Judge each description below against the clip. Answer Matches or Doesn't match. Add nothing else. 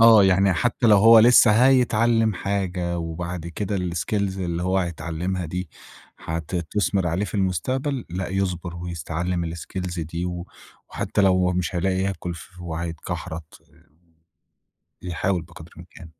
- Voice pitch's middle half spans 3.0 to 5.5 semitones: Doesn't match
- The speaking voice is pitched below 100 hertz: Matches